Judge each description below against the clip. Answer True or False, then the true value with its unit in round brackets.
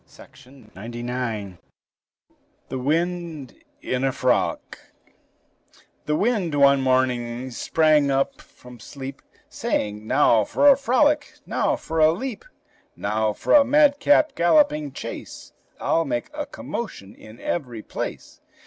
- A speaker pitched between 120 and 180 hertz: True (140 Hz)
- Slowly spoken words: True (120 wpm)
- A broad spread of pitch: True (8.2 semitones)